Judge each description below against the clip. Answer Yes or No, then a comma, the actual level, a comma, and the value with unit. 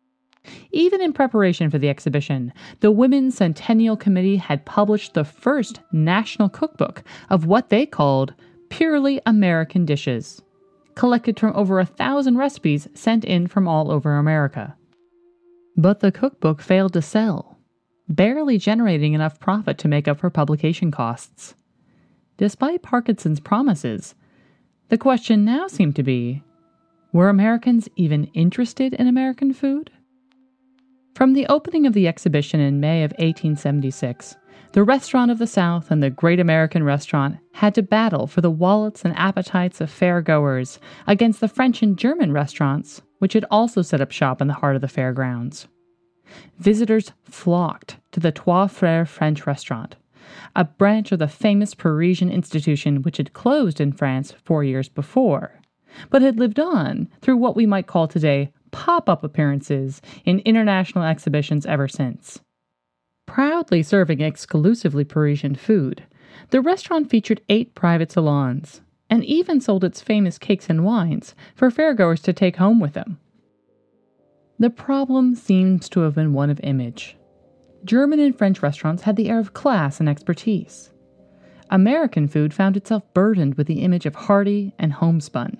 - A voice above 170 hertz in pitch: Yes, medium, 185 Hz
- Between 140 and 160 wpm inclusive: Yes, average, 150 wpm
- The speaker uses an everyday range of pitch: No, wide, 6.7 semitones